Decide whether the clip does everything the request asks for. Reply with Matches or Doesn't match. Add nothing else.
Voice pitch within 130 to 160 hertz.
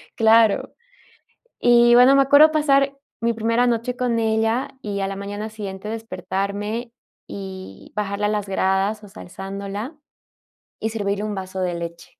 Doesn't match